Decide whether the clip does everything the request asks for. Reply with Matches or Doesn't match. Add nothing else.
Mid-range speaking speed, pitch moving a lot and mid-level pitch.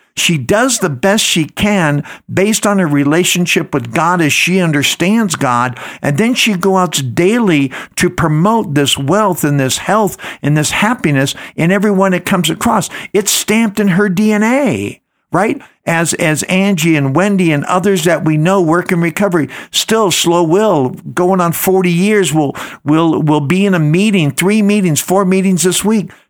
Doesn't match